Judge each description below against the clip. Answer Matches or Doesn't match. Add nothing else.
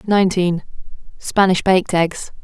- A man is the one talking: Doesn't match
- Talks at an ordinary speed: Doesn't match